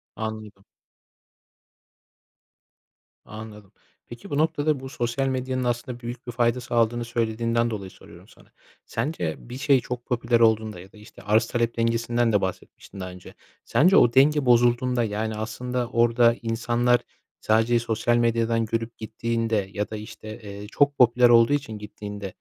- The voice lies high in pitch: No, low, 115 Hz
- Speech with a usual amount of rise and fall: No, narrow, 1.9 semitones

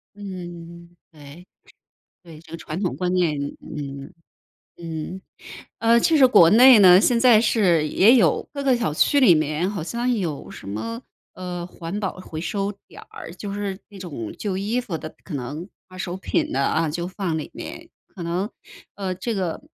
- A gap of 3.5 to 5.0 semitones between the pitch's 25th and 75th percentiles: Yes, average, 4.1 semitones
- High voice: No, medium, 180 Hz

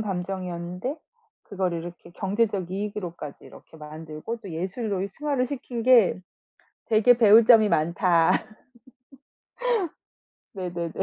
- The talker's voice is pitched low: No, high, 190 Hz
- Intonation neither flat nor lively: Yes, average, 4.5 semitones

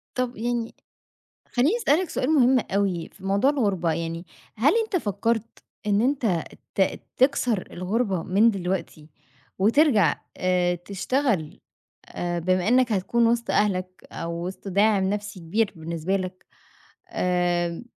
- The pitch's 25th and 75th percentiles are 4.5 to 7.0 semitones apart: Yes, average, 5.0 semitones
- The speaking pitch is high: Yes, high, 200 Hz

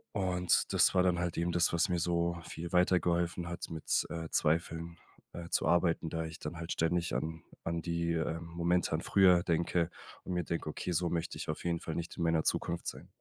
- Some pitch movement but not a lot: No, narrow, 1.0 semitones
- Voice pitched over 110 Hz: No, very low, 85 Hz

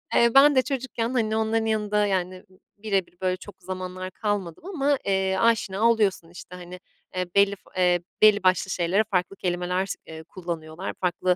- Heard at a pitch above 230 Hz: No, high, 190 Hz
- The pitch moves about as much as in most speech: Yes, average, 3.2 semitones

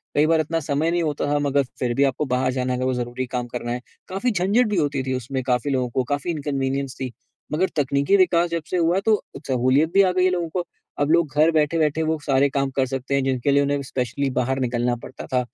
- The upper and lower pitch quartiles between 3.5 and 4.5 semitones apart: Yes, average, 4.1 semitones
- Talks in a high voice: No, medium, 140 Hz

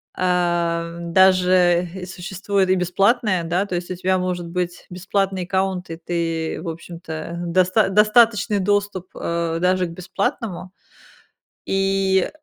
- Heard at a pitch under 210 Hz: Yes, medium, 185 Hz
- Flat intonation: Yes, narrow, 2.0 semitones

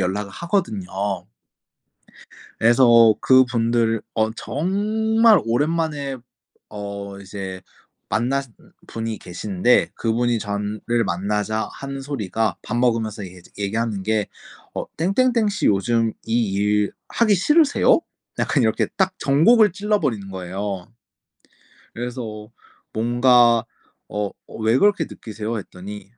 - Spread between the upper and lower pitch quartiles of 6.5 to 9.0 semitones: No, average, 5.3 semitones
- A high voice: No, low, 115 Hz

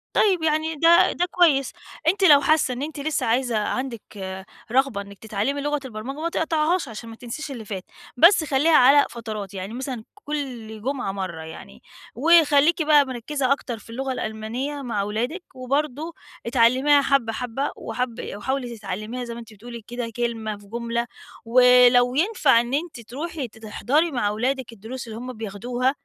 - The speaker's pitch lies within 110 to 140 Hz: No, very high, 250 Hz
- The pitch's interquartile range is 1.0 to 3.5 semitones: No, average, 4.4 semitones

